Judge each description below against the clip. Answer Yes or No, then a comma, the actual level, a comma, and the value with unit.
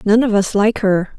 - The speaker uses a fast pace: Yes, fast, 255 wpm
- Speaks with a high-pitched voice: Yes, high, 210 Hz